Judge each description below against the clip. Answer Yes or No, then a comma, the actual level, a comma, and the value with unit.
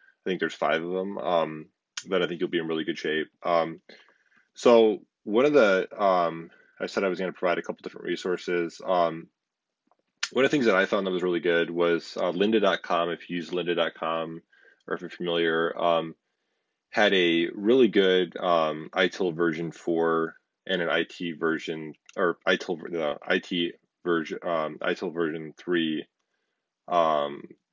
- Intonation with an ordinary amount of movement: No, narrow, 1.2 semitones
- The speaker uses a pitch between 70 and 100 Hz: Yes, very low, 85 Hz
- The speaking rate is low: No, average, 175 wpm